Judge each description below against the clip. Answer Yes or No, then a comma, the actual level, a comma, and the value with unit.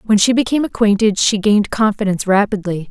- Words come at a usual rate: Yes, average, 165 wpm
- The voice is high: Yes, high, 210 Hz